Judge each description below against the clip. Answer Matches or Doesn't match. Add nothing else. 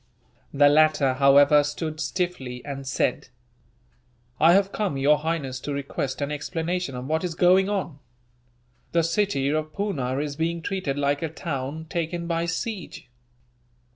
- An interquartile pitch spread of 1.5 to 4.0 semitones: Matches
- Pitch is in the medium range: Matches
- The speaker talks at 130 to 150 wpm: Matches